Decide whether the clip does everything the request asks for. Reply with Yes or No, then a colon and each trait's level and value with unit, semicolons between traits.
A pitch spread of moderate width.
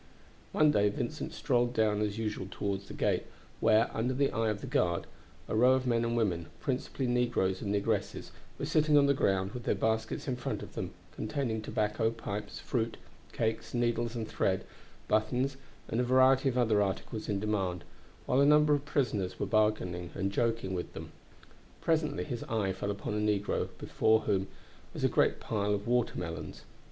Yes: average, 3.4 semitones